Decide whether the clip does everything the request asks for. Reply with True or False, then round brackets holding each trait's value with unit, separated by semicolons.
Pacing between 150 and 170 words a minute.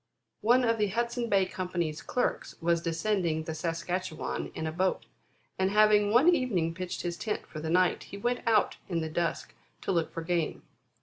False (185 wpm)